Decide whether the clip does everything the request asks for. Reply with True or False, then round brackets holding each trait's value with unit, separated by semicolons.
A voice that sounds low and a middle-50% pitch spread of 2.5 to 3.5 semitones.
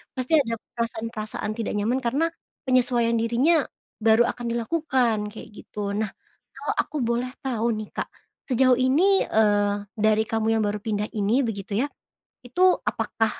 False (230 Hz; 2.9 semitones)